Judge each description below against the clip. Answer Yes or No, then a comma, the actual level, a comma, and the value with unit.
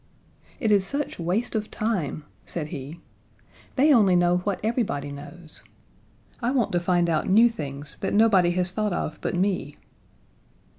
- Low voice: No, medium, 180 Hz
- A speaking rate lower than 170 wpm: Yes, average, 155 wpm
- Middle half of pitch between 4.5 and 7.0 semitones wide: Yes, average, 5.0 semitones